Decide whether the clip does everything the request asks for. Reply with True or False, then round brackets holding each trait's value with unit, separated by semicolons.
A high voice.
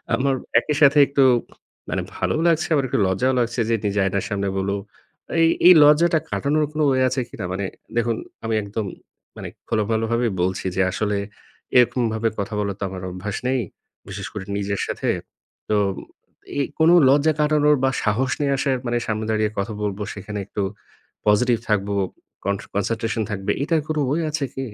False (115 Hz)